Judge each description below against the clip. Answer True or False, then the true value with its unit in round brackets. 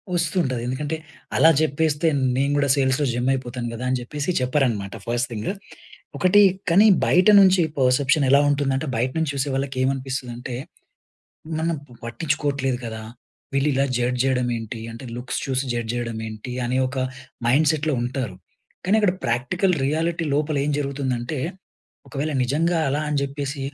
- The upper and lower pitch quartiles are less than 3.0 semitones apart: False (3.3 semitones)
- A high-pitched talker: False (135 Hz)